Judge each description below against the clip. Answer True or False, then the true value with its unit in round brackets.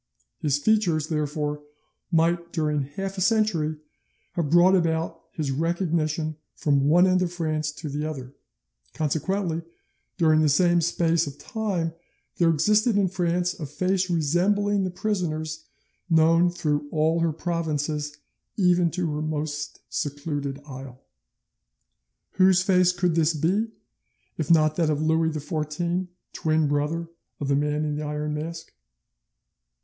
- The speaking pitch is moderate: True (160 Hz)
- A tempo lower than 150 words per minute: True (135 wpm)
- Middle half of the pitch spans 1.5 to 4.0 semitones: True (2.8 semitones)